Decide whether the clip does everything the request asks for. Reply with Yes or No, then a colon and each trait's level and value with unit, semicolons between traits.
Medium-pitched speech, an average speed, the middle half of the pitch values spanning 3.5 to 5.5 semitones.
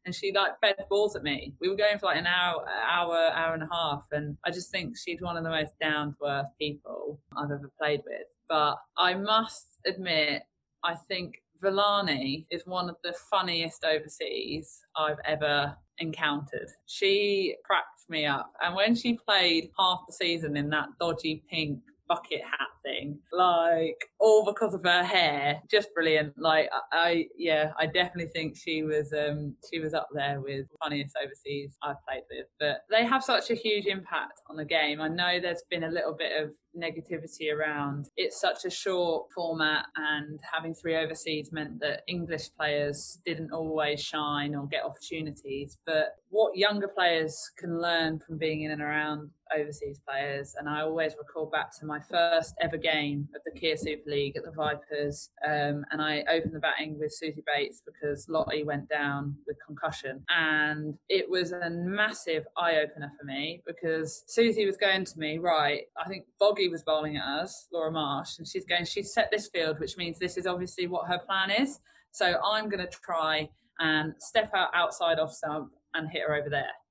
No: medium, 160 Hz; average, 185 wpm; average, 3.0 semitones